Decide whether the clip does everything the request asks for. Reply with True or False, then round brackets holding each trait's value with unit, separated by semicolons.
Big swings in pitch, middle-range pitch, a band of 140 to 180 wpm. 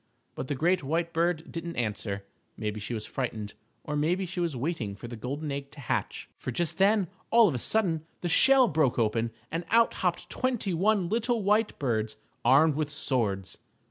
False (7.0 semitones; 155 Hz; 190 wpm)